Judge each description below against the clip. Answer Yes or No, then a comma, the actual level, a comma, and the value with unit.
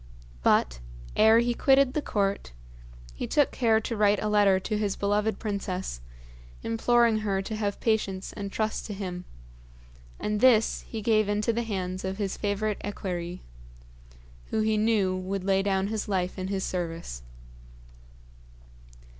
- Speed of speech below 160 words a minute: Yes, average, 150 wpm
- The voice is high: Yes, high, 205 Hz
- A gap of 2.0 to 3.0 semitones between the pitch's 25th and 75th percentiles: Yes, narrow, 2.4 semitones